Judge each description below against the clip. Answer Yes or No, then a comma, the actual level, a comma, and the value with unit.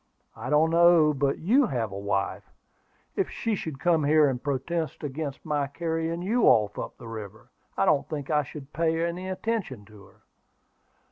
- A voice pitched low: No, medium, 150 Hz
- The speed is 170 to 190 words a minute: Yes, average, 180 wpm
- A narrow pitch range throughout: No, average, 4.4 semitones